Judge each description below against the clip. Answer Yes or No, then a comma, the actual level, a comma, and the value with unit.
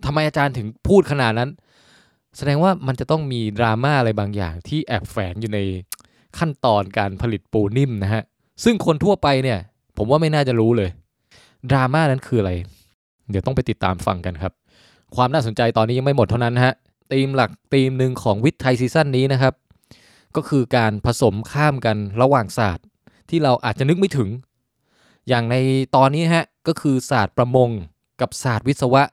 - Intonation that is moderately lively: Yes, average, 4.2 semitones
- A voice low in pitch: Yes, low, 125 Hz